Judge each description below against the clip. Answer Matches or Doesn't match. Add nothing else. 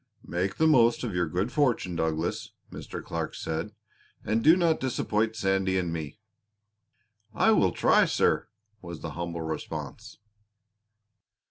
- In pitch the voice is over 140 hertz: Doesn't match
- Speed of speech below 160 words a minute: Matches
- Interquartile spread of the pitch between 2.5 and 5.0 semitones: Doesn't match